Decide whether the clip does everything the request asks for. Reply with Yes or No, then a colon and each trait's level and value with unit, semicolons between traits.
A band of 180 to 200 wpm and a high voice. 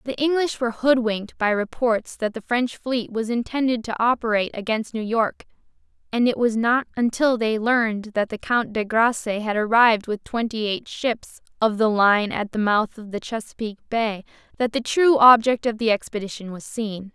Yes: average, 190 wpm; high, 225 Hz